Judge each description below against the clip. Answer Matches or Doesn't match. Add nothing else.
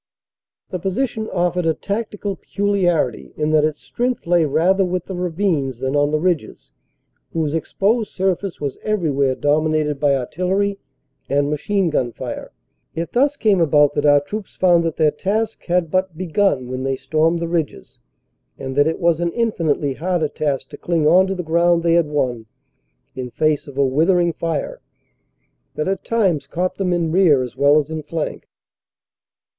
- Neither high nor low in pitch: Matches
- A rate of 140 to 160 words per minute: Doesn't match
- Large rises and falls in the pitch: Doesn't match